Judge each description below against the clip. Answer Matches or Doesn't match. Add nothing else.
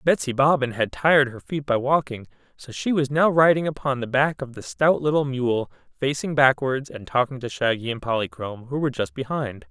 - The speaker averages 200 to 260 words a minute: Matches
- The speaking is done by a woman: Doesn't match